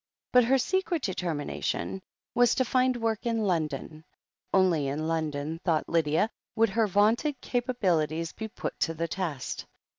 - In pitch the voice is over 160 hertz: Yes, high, 190 Hz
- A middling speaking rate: Yes, average, 145 wpm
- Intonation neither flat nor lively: No, wide, 6.9 semitones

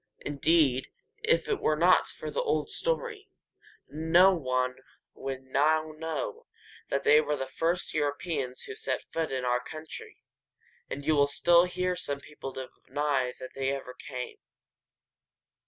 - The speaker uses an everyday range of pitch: Yes, average, 4.1 semitones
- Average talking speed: Yes, average, 145 wpm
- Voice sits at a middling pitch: Yes, medium, 150 Hz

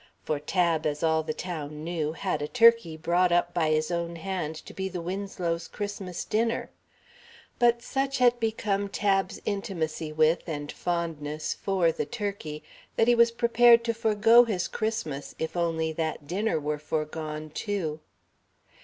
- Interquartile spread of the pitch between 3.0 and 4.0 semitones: No, average, 5.0 semitones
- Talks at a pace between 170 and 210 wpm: No, average, 155 wpm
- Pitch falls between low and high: Yes, medium, 175 Hz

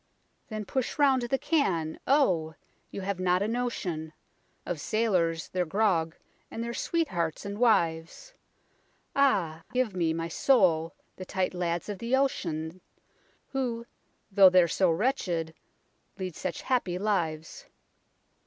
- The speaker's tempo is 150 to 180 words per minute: No, slow, 135 wpm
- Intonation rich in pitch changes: Yes, wide, 6.1 semitones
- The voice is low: No, medium, 185 Hz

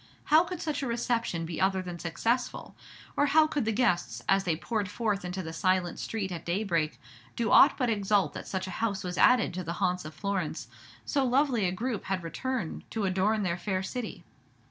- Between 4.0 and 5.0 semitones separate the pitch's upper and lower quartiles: Yes, average, 4.7 semitones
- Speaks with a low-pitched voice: No, high, 195 Hz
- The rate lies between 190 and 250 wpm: Yes, fast, 205 wpm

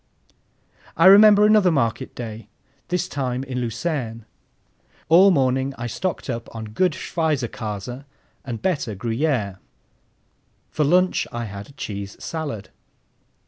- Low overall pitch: Yes, low, 130 Hz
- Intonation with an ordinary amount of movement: No, wide, 6.6 semitones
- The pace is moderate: No, slow, 115 wpm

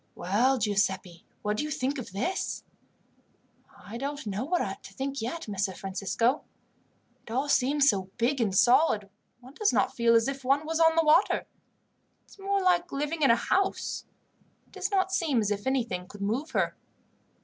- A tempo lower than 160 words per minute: No, average, 180 wpm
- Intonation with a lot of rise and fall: Yes, wide, 6.8 semitones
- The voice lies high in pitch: Yes, very high, 260 Hz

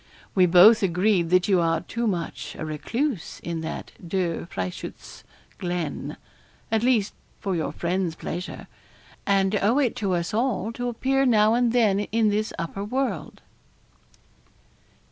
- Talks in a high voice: Yes, high, 195 Hz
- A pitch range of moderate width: Yes, average, 4.6 semitones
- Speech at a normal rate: Yes, average, 145 wpm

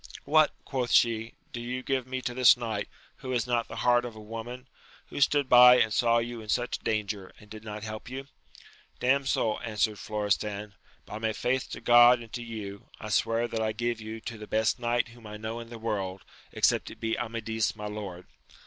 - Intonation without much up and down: Yes, narrow, 2.2 semitones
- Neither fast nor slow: No, fast, 210 wpm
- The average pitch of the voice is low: Yes, low, 115 Hz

